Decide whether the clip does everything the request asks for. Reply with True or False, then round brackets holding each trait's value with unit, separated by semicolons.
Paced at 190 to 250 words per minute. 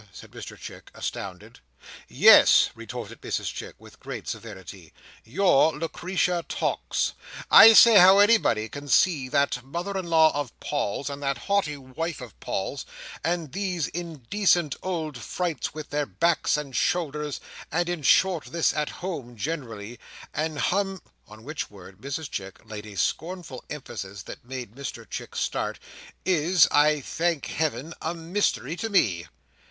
False (145 wpm)